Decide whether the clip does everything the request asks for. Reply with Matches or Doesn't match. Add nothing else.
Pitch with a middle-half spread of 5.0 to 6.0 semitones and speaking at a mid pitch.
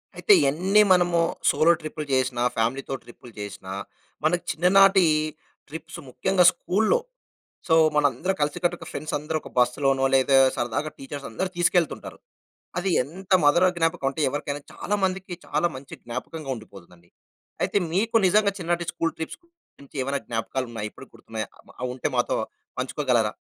Matches